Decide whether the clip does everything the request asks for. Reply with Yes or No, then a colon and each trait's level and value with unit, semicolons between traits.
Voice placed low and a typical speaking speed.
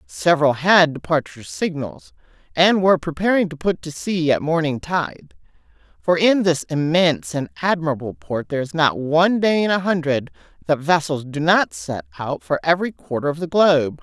No: medium, 165 Hz; average, 175 wpm